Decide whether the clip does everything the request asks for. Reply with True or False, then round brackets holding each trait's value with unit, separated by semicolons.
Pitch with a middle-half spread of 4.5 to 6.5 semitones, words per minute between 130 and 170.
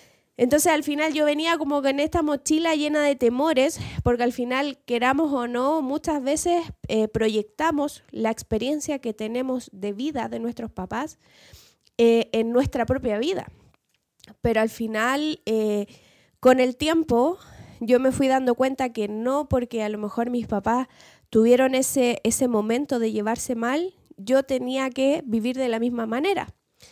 False (4.1 semitones; 160 wpm)